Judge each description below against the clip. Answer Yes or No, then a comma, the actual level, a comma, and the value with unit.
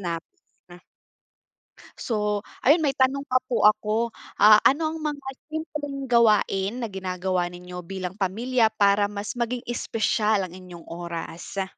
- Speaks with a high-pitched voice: Yes, high, 210 Hz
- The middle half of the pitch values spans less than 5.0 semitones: No, wide, 5.4 semitones